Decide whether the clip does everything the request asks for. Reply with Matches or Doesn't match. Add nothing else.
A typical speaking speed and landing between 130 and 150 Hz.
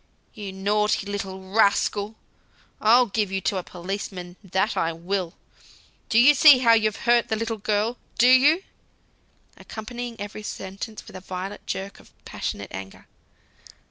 Doesn't match